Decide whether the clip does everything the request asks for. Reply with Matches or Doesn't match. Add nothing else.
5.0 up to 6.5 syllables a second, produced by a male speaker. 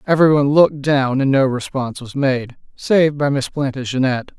Matches